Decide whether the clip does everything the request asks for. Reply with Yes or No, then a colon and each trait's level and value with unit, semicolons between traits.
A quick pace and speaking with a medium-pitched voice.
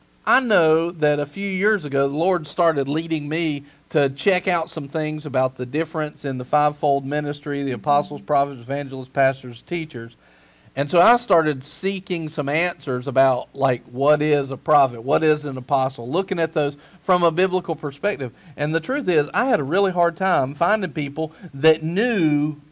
No: average, 180 wpm; medium, 150 Hz